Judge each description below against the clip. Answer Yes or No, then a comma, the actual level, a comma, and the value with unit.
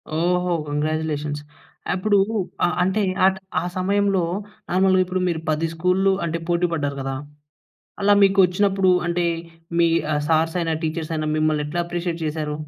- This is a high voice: No, medium, 170 Hz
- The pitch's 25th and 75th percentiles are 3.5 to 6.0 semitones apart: No, average, 3.0 semitones